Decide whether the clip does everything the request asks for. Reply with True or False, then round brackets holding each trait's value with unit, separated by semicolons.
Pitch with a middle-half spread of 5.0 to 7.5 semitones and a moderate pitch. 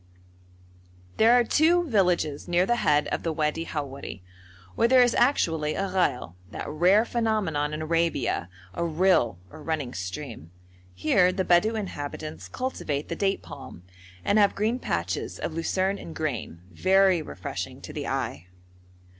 True (5.4 semitones; 170 Hz)